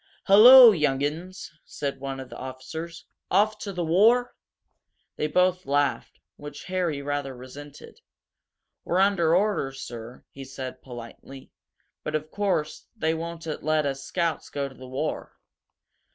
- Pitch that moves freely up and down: No, average, 5.0 semitones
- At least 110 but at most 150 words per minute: Yes, average, 140 wpm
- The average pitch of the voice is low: No, medium, 155 Hz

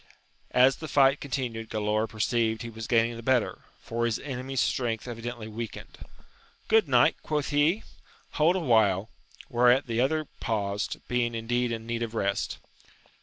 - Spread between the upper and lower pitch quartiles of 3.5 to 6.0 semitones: No, average, 2.8 semitones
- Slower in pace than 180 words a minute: Yes, average, 160 wpm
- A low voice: Yes, low, 120 Hz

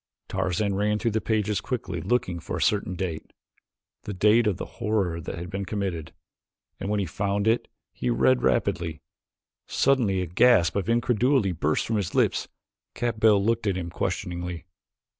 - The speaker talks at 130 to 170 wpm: Yes, average, 160 wpm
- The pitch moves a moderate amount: Yes, average, 3.9 semitones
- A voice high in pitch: No, low, 100 Hz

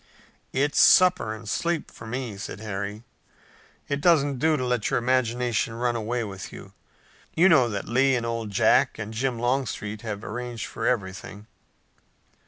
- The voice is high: No, low, 120 Hz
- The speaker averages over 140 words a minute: Yes, average, 160 wpm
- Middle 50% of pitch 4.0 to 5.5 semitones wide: No, average, 3.4 semitones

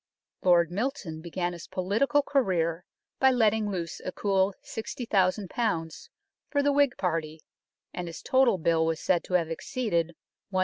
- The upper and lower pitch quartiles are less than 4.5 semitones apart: No, average, 5.3 semitones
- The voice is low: No, medium, 185 Hz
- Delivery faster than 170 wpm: No, average, 145 wpm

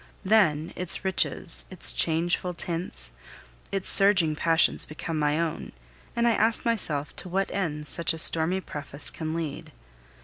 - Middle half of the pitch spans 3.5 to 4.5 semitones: Yes, average, 3.8 semitones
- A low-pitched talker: No, medium, 165 Hz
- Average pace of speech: Yes, average, 145 wpm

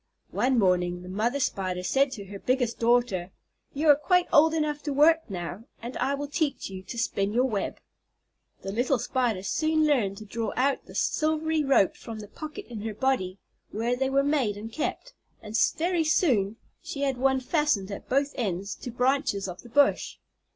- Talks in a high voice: Yes, high, 245 Hz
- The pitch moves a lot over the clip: Yes, wide, 6.0 semitones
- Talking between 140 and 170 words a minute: No, average, 190 wpm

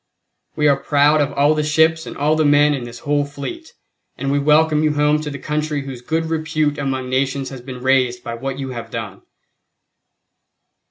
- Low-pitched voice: No, medium, 145 Hz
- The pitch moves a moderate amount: No, narrow, 2.2 semitones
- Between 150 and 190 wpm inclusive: No, average, 200 wpm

